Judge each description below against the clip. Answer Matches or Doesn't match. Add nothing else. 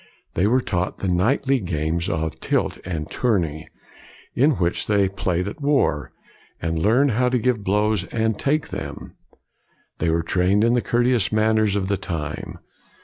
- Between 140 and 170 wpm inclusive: Matches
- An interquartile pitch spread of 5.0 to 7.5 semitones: Matches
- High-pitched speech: Doesn't match